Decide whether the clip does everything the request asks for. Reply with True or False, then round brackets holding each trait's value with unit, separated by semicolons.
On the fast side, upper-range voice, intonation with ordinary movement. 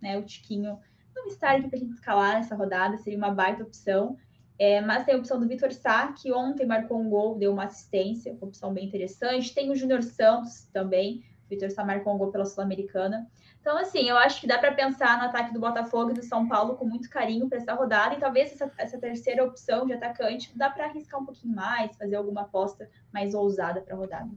True (230 wpm; 230 Hz; 4.2 semitones)